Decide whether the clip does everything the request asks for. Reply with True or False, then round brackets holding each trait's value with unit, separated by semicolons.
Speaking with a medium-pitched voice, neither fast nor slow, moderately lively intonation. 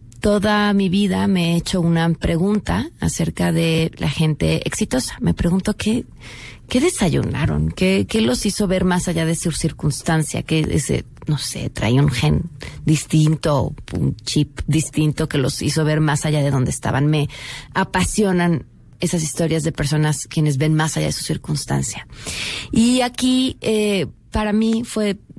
True (160 Hz; 160 wpm; 4.7 semitones)